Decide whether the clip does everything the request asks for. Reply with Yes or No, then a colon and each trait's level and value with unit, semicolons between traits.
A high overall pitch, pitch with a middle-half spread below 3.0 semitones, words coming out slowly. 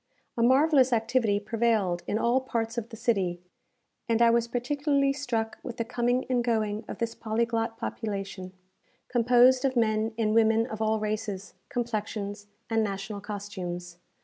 No: high, 225 Hz; narrow, 2.4 semitones; average, 150 wpm